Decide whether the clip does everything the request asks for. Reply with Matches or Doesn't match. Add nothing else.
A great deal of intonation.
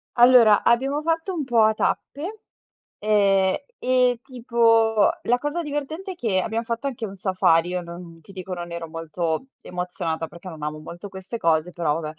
Matches